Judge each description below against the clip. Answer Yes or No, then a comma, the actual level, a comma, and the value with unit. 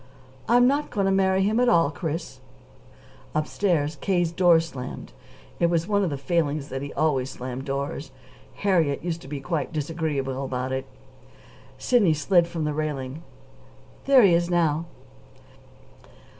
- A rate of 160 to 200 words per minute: No, average, 150 wpm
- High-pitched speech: No, medium, 160 Hz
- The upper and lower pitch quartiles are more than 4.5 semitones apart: No, average, 4.1 semitones